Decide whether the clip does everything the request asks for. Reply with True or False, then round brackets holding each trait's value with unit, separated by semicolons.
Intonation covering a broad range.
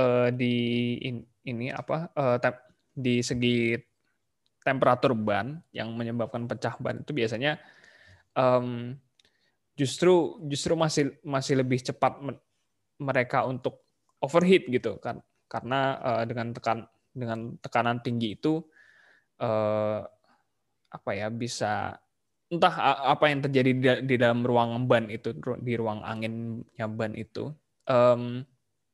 False (2.8 semitones)